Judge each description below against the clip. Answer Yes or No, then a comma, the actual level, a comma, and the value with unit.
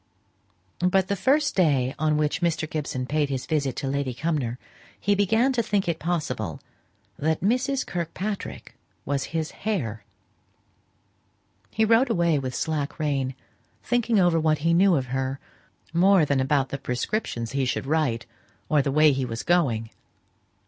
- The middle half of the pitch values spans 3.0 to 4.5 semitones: No, wide, 5.6 semitones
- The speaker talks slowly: No, average, 155 wpm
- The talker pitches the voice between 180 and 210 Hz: No, medium, 155 Hz